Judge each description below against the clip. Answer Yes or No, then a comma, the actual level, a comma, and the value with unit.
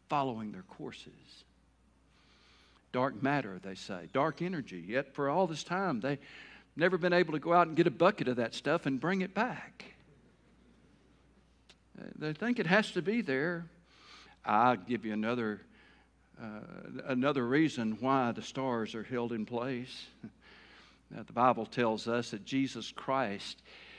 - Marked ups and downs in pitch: Yes, wide, 6.3 semitones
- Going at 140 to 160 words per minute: Yes, average, 155 wpm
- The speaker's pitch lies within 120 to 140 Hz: Yes, low, 135 Hz